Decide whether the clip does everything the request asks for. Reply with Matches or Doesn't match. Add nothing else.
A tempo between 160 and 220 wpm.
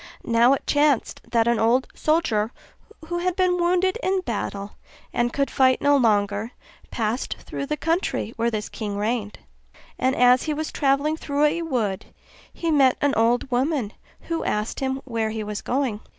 Matches